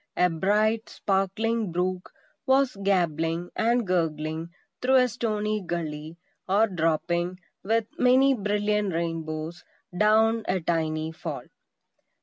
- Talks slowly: Yes, slow, 110 wpm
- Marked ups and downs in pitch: No, average, 4.8 semitones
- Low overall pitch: No, medium, 185 Hz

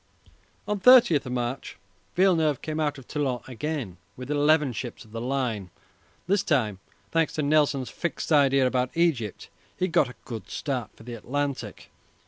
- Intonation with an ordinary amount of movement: Yes, average, 4.1 semitones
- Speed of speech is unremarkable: Yes, average, 155 wpm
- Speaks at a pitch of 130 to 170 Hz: Yes, medium, 140 Hz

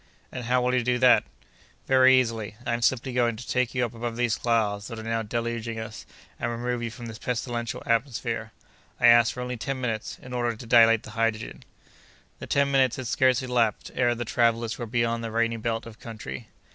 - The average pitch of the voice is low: Yes, low, 120 Hz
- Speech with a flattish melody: Yes, narrow, 1.5 semitones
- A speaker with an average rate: No, fast, 210 wpm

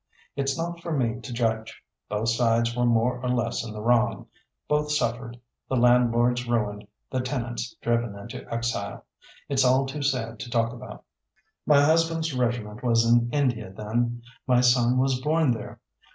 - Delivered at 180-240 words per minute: No, average, 165 wpm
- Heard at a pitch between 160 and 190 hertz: No, low, 120 Hz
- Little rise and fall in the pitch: Yes, narrow, 2.2 semitones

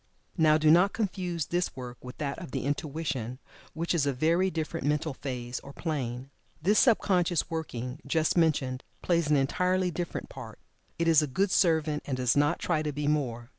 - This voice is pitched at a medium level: Yes, medium, 155 Hz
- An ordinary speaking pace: Yes, average, 190 wpm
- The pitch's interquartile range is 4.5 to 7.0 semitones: No, average, 3.9 semitones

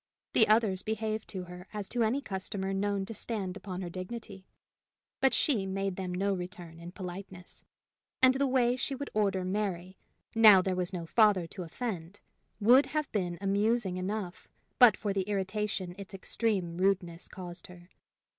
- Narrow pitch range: No, average, 3.0 semitones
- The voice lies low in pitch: No, high, 195 Hz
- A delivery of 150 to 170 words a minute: Yes, average, 165 wpm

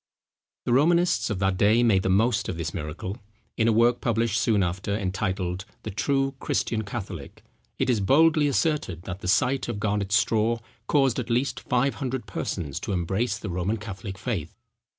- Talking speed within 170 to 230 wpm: Yes, average, 175 wpm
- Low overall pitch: Yes, low, 110 Hz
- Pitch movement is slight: No, average, 4.4 semitones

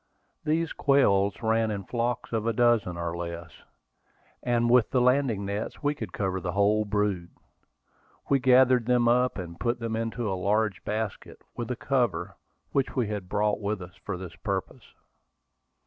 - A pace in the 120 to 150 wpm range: No, average, 165 wpm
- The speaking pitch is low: Yes, low, 110 Hz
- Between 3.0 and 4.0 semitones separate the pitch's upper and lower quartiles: Yes, average, 3.7 semitones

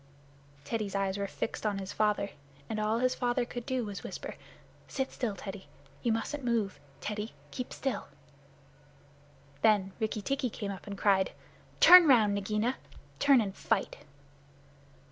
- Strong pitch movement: No, average, 3.4 semitones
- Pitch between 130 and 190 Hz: No, high, 215 Hz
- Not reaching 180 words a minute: Yes, average, 150 wpm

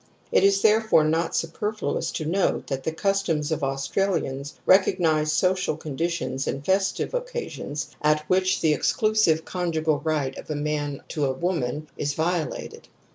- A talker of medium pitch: Yes, medium, 160 Hz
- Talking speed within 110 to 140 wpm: No, average, 150 wpm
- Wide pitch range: No, average, 4.1 semitones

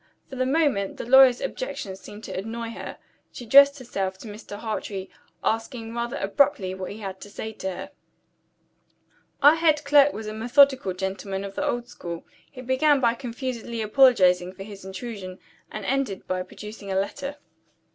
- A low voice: No, high, 225 Hz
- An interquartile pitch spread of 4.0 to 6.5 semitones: Yes, wide, 5.4 semitones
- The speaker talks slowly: No, average, 170 wpm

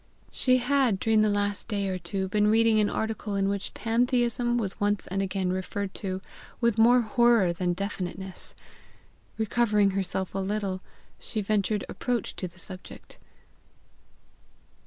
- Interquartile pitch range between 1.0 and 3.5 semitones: Yes, average, 2.9 semitones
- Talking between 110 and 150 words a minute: Yes, average, 145 wpm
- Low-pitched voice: No, high, 205 Hz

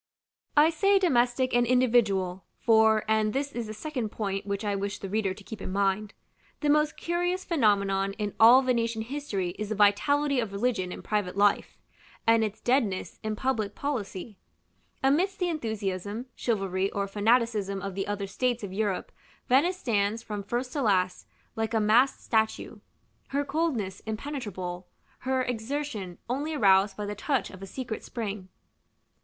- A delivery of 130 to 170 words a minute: Yes, average, 160 wpm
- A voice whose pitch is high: Yes, high, 220 Hz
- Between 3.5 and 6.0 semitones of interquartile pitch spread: Yes, average, 4.4 semitones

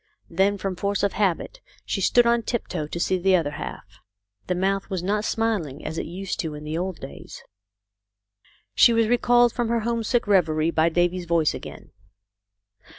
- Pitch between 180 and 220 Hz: Yes, high, 190 Hz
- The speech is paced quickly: No, average, 175 wpm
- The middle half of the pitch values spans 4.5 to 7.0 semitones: Yes, average, 5.0 semitones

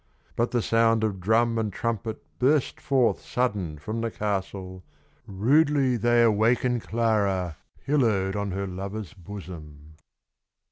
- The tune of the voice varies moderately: Yes, average, 3.6 semitones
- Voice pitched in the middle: No, low, 110 Hz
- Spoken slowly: Yes, slow, 125 wpm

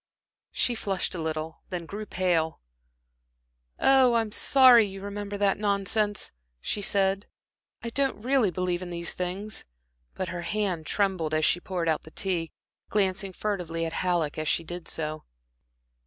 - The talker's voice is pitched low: No, high, 190 Hz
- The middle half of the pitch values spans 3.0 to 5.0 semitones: Yes, average, 3.5 semitones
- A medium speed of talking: Yes, average, 155 wpm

